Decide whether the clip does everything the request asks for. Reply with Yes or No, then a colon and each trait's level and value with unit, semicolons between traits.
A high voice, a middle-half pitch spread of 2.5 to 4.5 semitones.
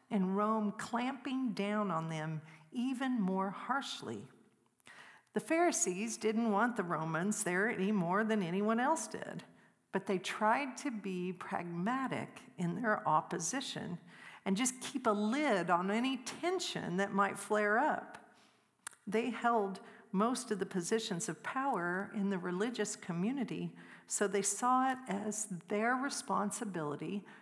Yes: high, 210 Hz; average, 3.8 semitones